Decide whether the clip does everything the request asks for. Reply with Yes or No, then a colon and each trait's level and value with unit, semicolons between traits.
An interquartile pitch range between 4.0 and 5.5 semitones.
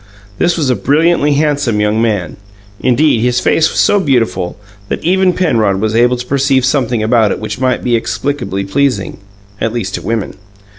Yes: average, 4.6 semitones